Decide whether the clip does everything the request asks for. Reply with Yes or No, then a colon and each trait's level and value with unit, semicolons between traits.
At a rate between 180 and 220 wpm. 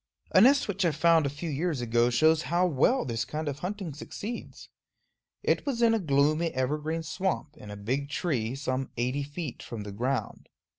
Yes: average, 190 wpm